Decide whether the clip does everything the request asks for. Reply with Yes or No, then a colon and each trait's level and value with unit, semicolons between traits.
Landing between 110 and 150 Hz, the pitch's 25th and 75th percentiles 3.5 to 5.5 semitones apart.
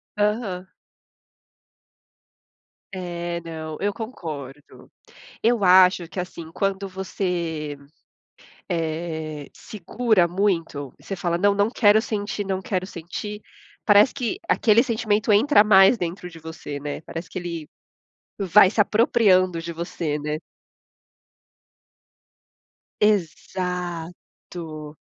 No: medium, 180 Hz; average, 3.8 semitones